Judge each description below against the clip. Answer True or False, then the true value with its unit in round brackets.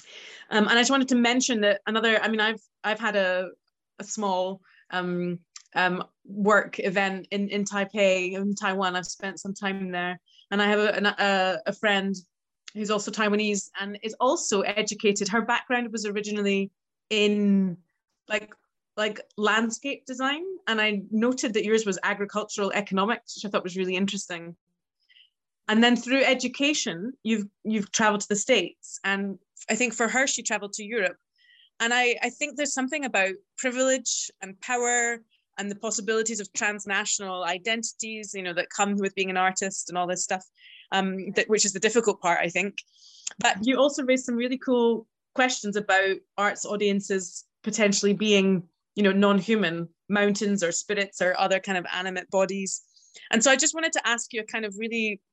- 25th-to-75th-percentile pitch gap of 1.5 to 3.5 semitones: True (2.9 semitones)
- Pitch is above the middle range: True (205 Hz)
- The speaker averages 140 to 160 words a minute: False (175 wpm)